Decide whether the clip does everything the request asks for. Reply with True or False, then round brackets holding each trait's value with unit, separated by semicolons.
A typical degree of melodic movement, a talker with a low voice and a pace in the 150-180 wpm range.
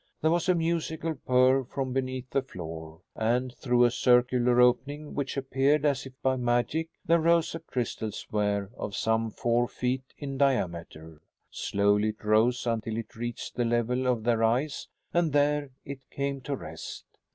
True (3.5 semitones; 125 Hz; 165 wpm)